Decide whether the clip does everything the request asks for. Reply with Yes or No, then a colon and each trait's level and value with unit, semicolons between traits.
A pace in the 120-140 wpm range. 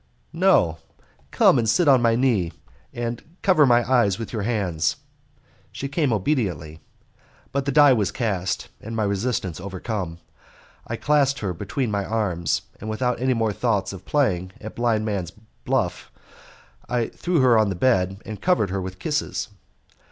No: average, 160 wpm